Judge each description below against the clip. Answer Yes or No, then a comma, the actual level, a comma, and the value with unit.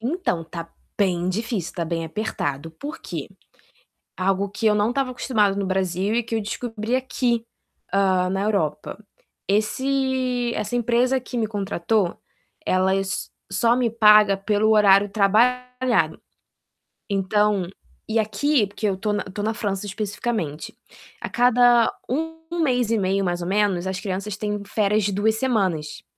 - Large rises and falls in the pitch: No, average, 3.7 semitones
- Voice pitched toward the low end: No, high, 210 Hz